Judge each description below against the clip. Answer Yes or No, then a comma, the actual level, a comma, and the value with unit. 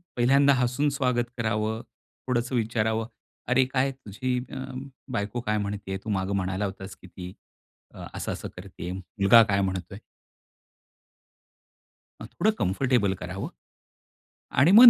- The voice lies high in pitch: No, low, 110 Hz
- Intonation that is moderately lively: Yes, average, 4.6 semitones